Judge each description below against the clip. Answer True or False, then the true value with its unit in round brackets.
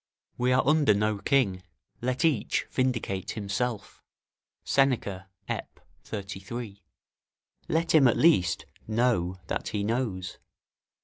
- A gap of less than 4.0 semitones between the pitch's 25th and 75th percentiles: False (4.7 semitones)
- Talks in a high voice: False (110 Hz)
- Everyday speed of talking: False (105 wpm)